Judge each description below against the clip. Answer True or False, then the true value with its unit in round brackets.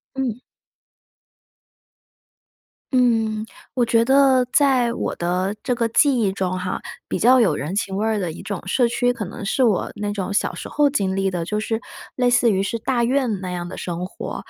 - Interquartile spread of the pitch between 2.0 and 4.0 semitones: False (4.5 semitones)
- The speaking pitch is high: True (220 Hz)